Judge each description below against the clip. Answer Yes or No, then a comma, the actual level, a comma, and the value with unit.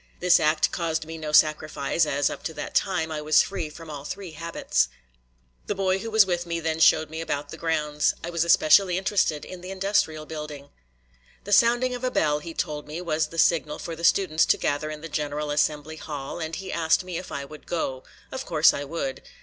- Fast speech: Yes, fast, 220 wpm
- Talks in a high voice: No, medium, 160 Hz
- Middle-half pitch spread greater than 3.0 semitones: No, average, 2.7 semitones